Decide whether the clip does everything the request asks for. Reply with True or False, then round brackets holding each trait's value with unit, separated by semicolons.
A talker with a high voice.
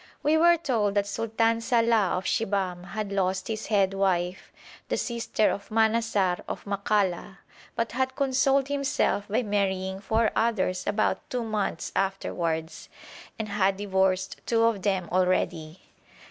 True (205 Hz)